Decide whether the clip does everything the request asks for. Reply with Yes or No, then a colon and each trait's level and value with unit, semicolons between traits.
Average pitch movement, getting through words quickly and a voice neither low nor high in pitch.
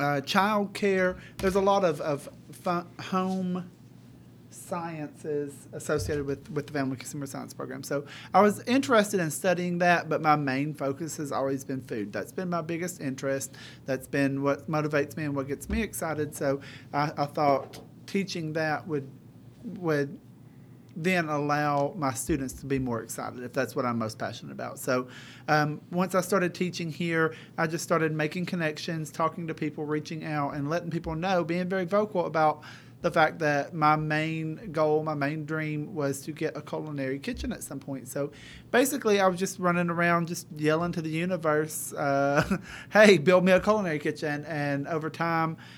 No: average, 3.7 semitones; average, 180 wpm; medium, 155 Hz